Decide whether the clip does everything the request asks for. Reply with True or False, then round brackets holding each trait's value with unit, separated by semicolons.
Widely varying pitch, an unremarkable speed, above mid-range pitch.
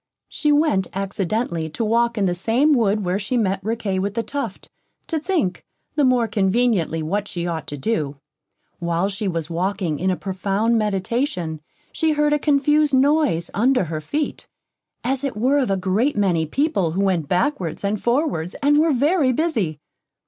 True (6.9 semitones; 175 wpm; 210 Hz)